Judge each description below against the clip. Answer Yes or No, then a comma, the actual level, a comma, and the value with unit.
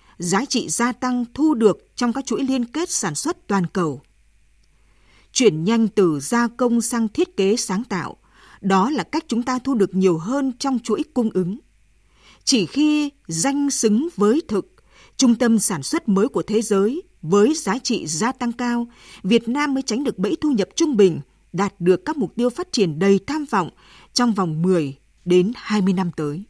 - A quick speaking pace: No, average, 190 wpm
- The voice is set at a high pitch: Yes, high, 220 Hz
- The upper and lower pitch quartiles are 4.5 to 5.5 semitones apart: Yes, average, 5.2 semitones